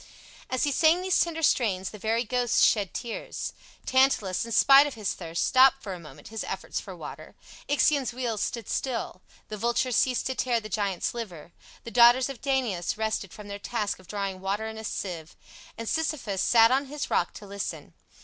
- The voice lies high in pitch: Yes, high, 230 Hz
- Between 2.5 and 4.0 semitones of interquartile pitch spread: No, average, 4.5 semitones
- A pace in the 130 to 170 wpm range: No, average, 195 wpm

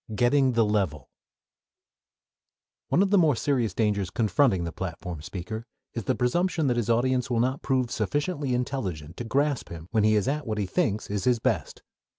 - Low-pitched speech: Yes, low, 115 Hz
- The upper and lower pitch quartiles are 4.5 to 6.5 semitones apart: Yes, average, 4.9 semitones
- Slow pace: No, average, 185 wpm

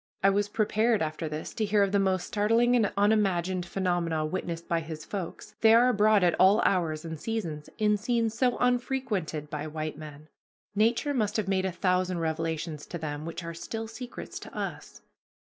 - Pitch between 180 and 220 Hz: Yes, high, 190 Hz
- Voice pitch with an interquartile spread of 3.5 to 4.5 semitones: No, average, 4.9 semitones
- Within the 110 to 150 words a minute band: No, average, 185 wpm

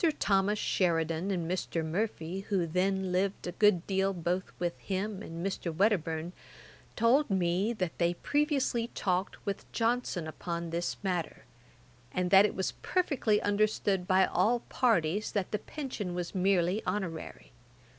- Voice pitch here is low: No, high, 190 Hz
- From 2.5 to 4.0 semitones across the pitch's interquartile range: Yes, average, 3.2 semitones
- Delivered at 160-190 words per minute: No, average, 145 wpm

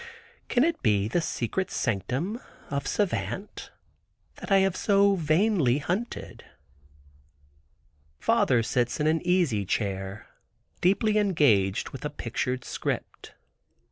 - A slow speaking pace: Yes, slow, 110 wpm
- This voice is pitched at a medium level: Yes, medium, 155 Hz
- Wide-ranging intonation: Yes, wide, 8.9 semitones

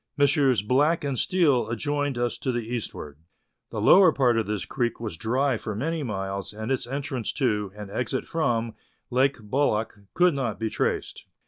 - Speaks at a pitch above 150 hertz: No, low, 125 Hz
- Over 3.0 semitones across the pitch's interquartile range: Yes, average, 4.4 semitones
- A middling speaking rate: Yes, average, 175 wpm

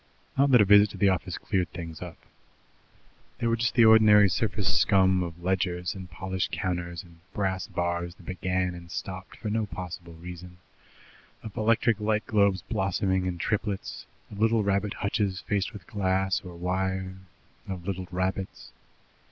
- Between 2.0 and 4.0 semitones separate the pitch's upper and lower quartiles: Yes, narrow, 2.5 semitones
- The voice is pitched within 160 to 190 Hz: No, very low, 95 Hz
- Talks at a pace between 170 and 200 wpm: No, average, 160 wpm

